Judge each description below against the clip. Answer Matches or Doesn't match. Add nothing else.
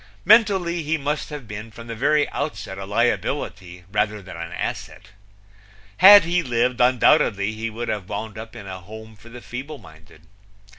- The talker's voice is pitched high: Doesn't match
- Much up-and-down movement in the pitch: Matches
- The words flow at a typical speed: Matches